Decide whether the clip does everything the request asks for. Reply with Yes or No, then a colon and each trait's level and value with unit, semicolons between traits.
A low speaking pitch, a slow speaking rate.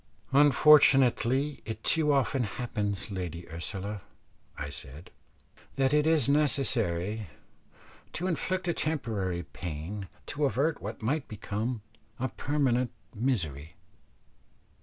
Yes: low, 120 Hz; slow, 105 wpm